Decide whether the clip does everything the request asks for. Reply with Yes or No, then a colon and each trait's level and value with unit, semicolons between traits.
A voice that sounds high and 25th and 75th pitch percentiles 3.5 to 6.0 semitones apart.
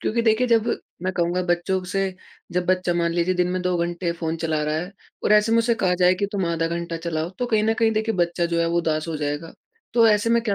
No: medium, 180 Hz; average, 3.9 semitones